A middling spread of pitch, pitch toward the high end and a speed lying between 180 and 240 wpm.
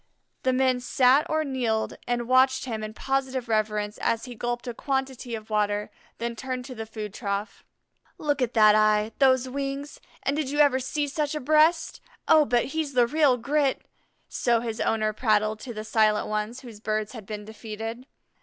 Yes: average, 3.7 semitones; high, 240 Hz; average, 185 wpm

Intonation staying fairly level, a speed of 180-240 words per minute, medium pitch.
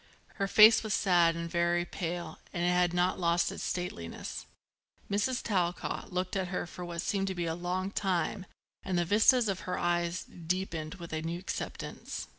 Yes: narrow, 2.0 semitones; average, 185 wpm; medium, 175 Hz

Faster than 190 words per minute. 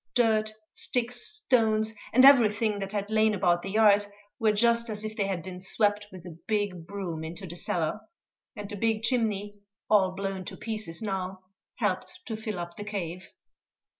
No: average, 175 wpm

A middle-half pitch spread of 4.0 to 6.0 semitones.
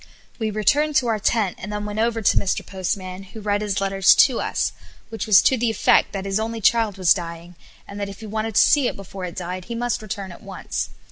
No: average, 2.7 semitones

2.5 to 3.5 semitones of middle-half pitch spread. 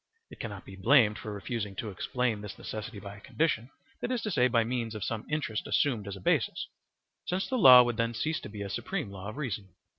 No: average, 4.0 semitones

